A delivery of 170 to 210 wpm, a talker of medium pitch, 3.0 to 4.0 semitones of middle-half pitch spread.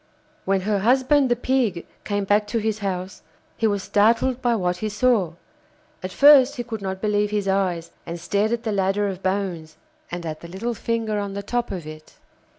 No: average, 200 wpm; high, 205 Hz; average, 3.4 semitones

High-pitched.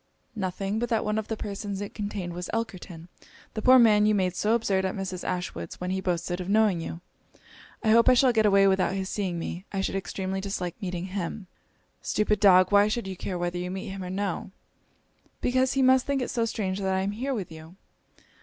Yes: high, 195 Hz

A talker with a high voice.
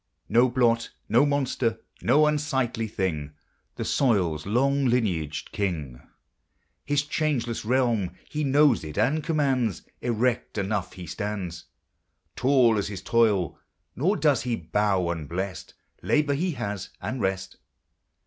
No: low, 115 Hz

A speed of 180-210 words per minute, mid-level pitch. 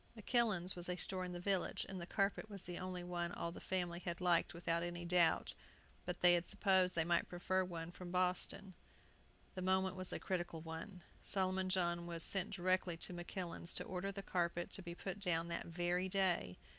Yes: average, 200 wpm; medium, 180 Hz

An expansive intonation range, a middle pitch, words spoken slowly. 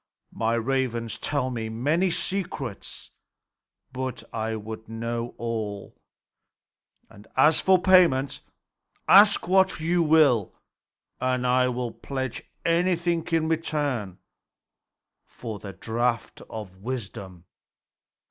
No: wide, 6.2 semitones; low, 125 Hz; slow, 100 wpm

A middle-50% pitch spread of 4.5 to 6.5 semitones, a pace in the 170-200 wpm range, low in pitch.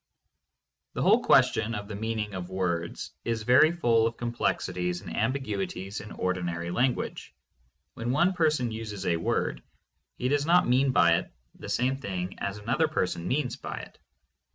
No: wide, 5.5 semitones; average, 160 wpm; low, 110 Hz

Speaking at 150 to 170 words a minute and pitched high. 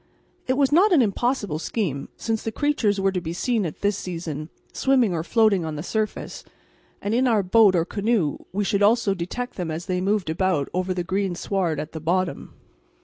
No: fast, 205 wpm; high, 195 Hz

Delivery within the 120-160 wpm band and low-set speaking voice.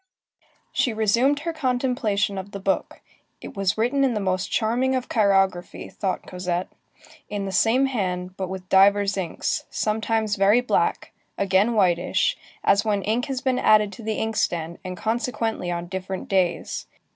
No: average, 155 wpm; high, 205 Hz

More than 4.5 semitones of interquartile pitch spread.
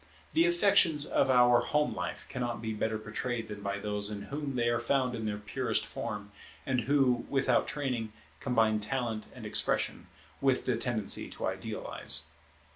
No: average, 3.9 semitones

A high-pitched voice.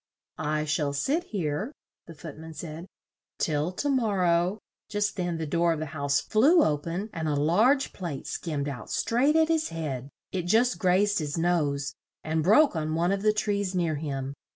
No: medium, 170 Hz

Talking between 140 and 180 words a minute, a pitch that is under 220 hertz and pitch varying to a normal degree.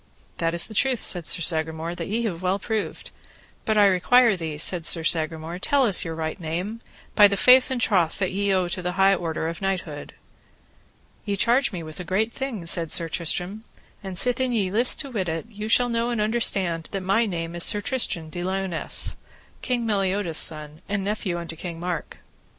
No: average, 200 wpm; high, 190 Hz; average, 4.5 semitones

